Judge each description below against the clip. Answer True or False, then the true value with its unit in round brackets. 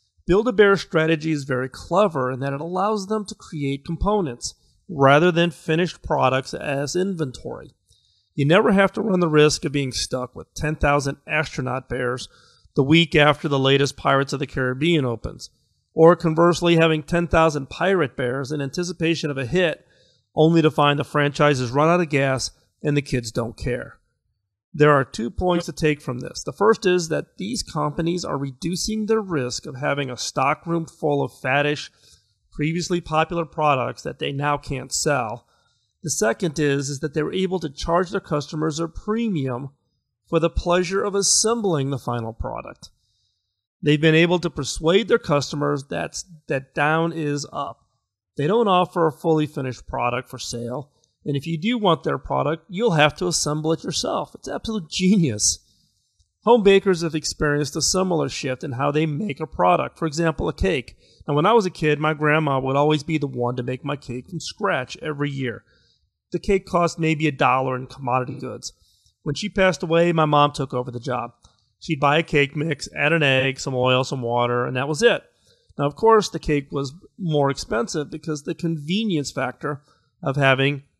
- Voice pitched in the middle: True (150 Hz)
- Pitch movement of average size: True (4.2 semitones)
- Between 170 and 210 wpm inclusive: True (185 wpm)